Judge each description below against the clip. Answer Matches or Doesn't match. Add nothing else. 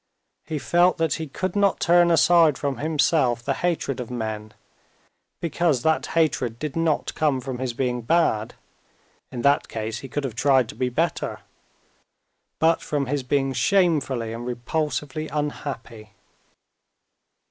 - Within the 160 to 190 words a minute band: Doesn't match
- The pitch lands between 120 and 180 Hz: Matches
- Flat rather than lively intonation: Doesn't match